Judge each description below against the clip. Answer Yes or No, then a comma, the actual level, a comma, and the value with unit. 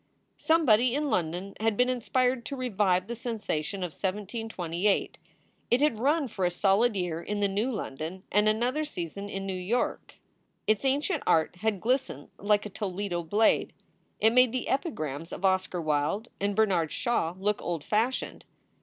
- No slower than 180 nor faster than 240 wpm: No, average, 165 wpm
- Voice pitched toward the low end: No, high, 205 Hz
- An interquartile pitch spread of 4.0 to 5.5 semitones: Yes, average, 5.0 semitones